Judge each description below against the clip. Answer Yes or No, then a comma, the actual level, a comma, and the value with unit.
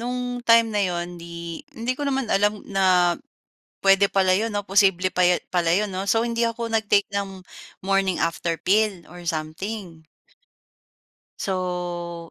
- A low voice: No, high, 195 Hz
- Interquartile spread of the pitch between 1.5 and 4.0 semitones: Yes, average, 3.7 semitones